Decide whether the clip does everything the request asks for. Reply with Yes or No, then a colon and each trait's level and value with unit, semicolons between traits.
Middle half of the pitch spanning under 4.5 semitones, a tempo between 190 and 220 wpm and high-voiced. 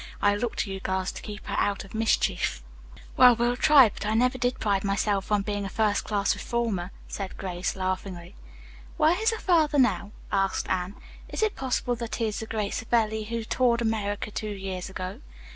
Yes: average, 3.4 semitones; average, 195 wpm; high, 210 Hz